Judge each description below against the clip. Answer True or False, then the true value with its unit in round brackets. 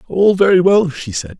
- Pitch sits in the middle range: True (170 Hz)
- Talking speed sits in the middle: False (215 wpm)